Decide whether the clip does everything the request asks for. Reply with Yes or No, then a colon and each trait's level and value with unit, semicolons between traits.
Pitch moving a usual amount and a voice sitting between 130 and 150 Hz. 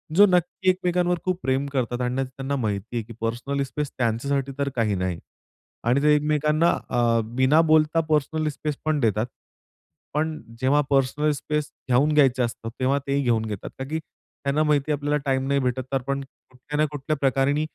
Yes: average, 3.3 semitones; medium, 140 Hz